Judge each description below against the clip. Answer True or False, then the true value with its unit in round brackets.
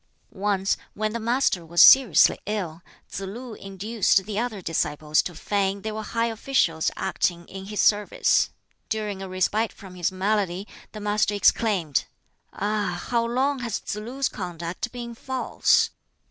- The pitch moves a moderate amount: True (3.5 semitones)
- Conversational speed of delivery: True (150 wpm)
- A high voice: True (205 Hz)